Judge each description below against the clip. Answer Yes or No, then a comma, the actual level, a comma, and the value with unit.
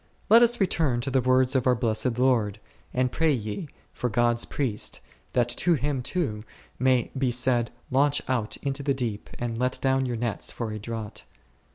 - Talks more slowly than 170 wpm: No, average, 185 wpm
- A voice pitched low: Yes, low, 125 Hz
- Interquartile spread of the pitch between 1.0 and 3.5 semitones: Yes, narrow, 2.5 semitones